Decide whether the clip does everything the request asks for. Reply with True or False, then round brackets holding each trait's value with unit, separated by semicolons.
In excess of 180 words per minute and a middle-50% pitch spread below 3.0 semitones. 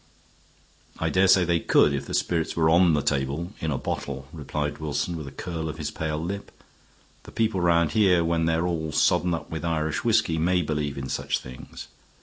True (200 wpm; 2.6 semitones)